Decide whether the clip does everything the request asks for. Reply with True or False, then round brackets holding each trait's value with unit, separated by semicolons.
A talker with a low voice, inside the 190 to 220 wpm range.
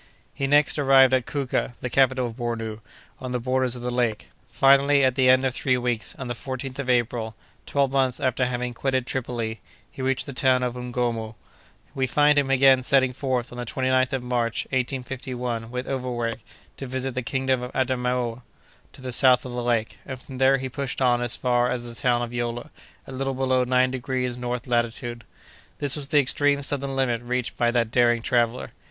True (125 Hz; 200 wpm)